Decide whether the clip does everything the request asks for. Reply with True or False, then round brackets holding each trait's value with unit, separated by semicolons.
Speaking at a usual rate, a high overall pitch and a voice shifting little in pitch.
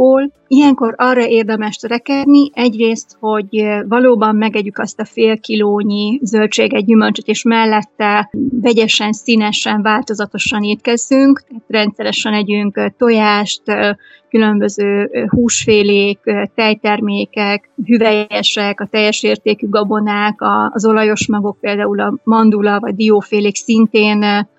False (100 wpm; 215 Hz; 1.9 semitones)